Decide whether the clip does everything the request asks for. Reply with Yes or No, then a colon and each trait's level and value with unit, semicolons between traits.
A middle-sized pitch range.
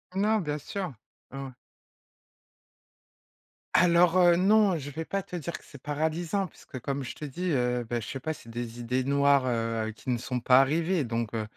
No: wide, 5.8 semitones